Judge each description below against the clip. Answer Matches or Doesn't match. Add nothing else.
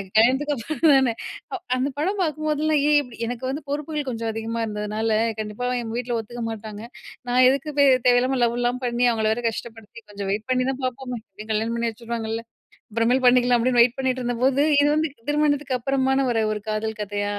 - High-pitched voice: Matches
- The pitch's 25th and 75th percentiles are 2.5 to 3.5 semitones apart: Matches